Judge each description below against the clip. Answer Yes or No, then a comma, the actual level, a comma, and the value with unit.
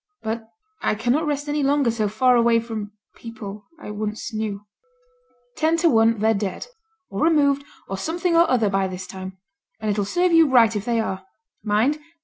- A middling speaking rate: Yes, average, 180 wpm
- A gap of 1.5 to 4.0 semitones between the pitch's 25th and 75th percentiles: No, average, 5.3 semitones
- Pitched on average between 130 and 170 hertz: No, high, 225 Hz